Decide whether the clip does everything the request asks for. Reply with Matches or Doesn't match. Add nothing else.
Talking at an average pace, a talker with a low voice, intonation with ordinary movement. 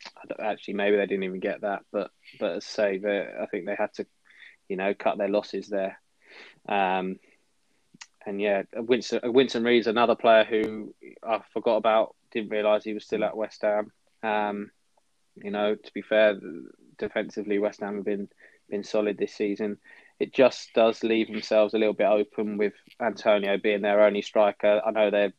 Doesn't match